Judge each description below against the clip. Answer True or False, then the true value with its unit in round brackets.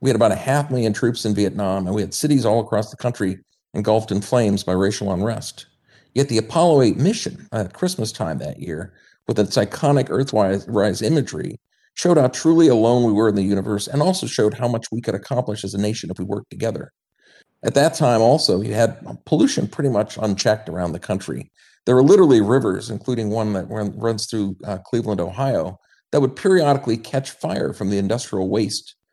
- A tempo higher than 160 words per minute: True (195 wpm)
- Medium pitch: False (110 Hz)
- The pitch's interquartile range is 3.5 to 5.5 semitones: True (4.1 semitones)